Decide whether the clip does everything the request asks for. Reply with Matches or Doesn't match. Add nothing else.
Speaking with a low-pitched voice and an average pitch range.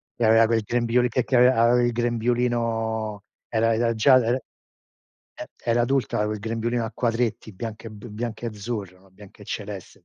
Doesn't match